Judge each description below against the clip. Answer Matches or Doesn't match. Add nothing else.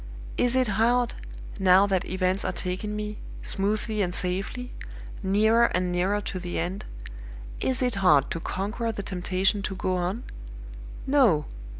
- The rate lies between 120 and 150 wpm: Matches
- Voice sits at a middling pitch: Doesn't match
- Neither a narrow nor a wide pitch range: Matches